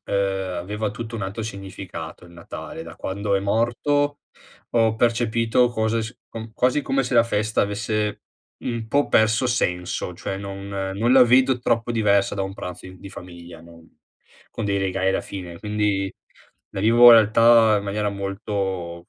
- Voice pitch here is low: Yes, low, 105 Hz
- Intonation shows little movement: No, average, 3.1 semitones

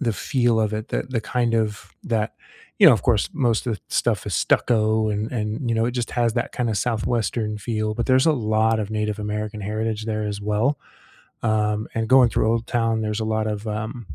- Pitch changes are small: Yes, narrow, 1.7 semitones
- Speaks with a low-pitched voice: Yes, low, 110 Hz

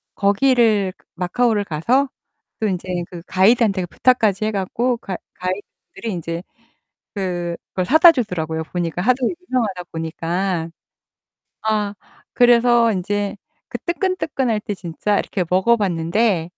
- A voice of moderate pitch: No, high, 200 Hz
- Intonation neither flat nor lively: Yes, average, 4.7 semitones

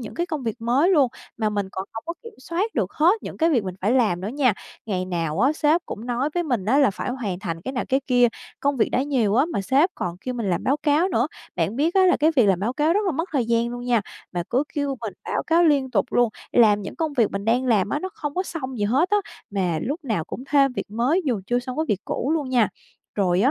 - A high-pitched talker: Yes, very high, 250 Hz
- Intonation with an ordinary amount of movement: No, wide, 5.9 semitones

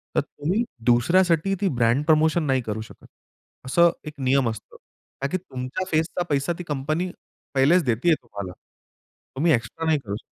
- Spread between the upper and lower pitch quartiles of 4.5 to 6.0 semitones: Yes, average, 5.3 semitones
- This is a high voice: No, medium, 145 Hz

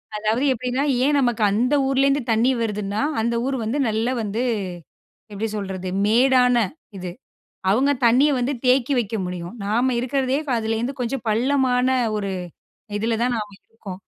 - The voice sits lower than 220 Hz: No, high, 235 Hz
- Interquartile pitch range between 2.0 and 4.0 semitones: Yes, average, 3.4 semitones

